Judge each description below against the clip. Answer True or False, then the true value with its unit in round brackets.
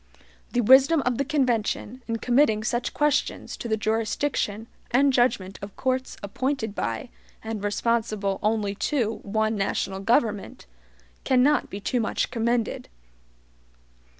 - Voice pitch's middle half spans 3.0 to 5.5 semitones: True (3.6 semitones)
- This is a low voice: False (225 Hz)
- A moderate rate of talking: False (125 wpm)